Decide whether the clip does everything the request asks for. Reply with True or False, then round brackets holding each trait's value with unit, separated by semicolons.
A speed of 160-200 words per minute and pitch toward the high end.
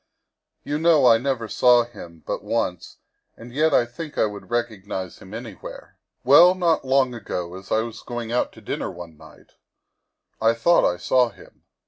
False (180 wpm; 120 Hz)